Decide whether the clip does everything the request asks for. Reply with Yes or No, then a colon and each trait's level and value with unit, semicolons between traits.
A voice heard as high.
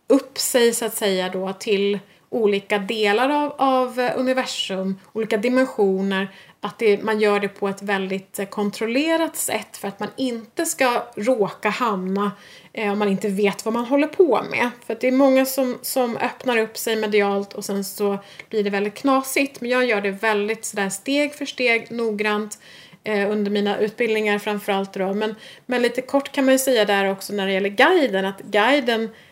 Yes: high, 215 Hz